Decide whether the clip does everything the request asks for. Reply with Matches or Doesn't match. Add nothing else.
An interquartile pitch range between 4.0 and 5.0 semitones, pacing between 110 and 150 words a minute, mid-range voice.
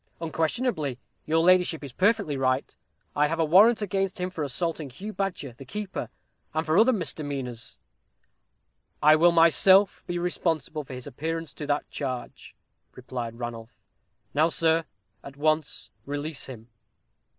Matches